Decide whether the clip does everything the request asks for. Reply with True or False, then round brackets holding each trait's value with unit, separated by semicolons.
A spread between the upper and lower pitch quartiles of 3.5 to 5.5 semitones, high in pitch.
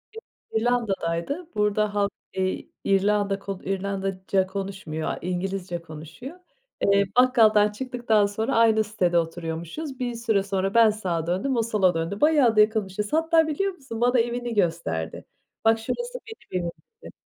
True (4.1 semitones; 205 Hz)